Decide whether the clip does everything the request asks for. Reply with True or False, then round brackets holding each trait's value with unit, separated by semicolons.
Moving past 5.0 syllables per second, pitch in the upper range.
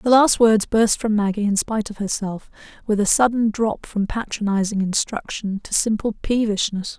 False (4.9 syllables/s; 215 Hz)